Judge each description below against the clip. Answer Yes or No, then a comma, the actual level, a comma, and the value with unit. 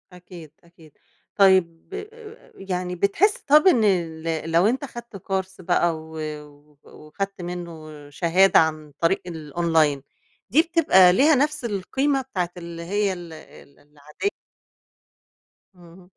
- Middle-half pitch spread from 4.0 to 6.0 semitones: No, average, 3.5 semitones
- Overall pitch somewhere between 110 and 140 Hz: No, medium, 180 Hz